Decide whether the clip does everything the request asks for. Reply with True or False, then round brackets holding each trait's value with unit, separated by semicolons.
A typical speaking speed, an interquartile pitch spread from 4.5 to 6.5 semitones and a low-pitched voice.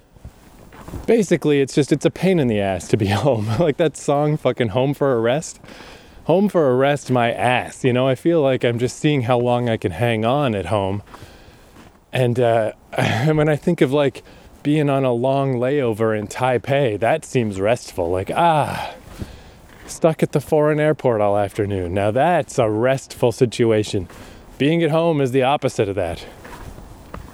True (180 wpm; 5.2 semitones; 125 Hz)